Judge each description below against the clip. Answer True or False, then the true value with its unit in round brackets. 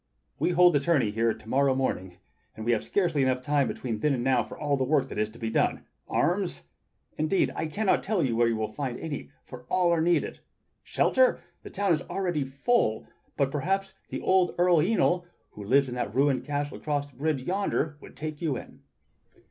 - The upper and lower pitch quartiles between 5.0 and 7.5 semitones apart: True (5.5 semitones)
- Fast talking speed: True (210 wpm)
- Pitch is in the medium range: True (145 Hz)